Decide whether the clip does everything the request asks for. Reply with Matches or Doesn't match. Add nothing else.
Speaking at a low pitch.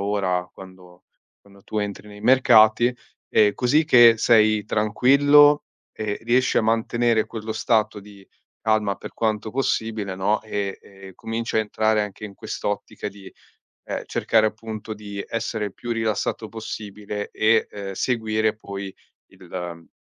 Matches